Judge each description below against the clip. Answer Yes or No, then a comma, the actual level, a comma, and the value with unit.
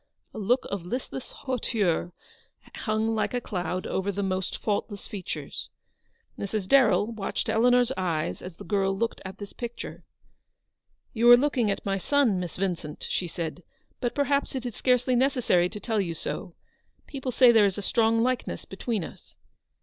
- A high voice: Yes, high, 215 Hz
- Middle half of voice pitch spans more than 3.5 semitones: Yes, average, 4.5 semitones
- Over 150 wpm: Yes, average, 175 wpm